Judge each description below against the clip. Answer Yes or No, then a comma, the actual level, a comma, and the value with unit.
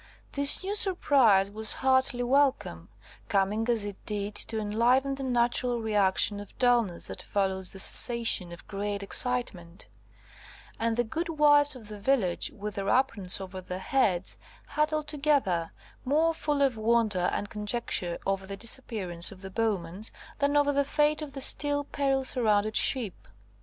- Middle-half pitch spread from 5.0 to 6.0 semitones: Yes, wide, 5.6 semitones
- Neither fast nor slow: Yes, average, 155 wpm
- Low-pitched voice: No, high, 230 Hz